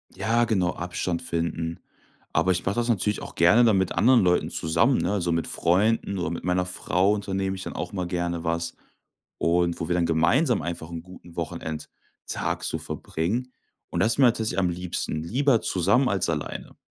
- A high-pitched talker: No, very low, 90 Hz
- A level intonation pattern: No, average, 3.8 semitones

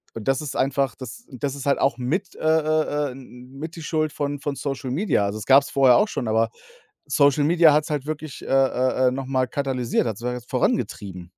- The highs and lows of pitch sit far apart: No, average, 2.9 semitones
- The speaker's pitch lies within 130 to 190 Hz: Yes, low, 135 Hz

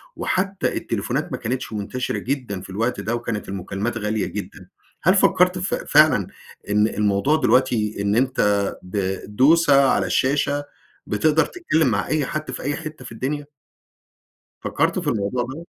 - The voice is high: No, low, 125 Hz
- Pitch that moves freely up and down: Yes, wide, 6.3 semitones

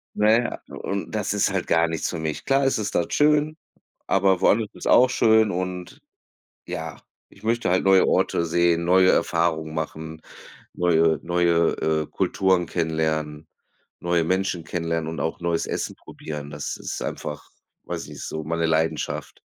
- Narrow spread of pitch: No, average, 3.2 semitones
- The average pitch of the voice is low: Yes, very low, 85 Hz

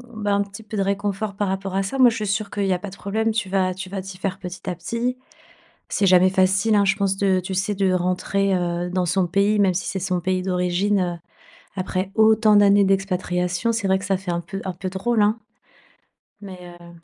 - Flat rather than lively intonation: Yes, narrow, 1.8 semitones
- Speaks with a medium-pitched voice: No, high, 195 Hz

